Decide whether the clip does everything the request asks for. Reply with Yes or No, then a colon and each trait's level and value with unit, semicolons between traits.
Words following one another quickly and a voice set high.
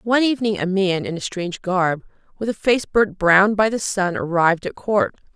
Yes: fast, 215 wpm; high, 195 Hz